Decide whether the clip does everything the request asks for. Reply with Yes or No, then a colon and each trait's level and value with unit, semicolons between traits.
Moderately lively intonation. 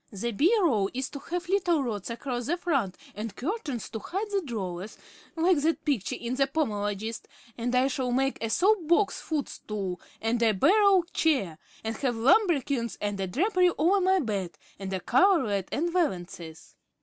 No: wide, 8.4 semitones